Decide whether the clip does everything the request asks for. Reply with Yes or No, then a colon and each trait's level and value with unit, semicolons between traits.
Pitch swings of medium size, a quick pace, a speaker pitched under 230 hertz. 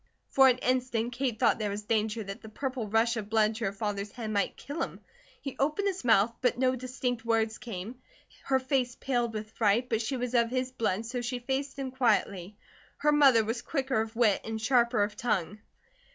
No: average, 3.0 semitones; fast, 210 wpm; high, 235 Hz